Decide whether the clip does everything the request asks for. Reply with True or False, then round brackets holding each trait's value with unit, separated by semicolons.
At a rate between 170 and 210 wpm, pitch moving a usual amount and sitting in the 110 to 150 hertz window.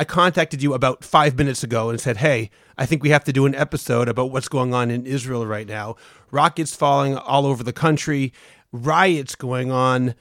True (205 wpm; 3.2 semitones; 135 Hz)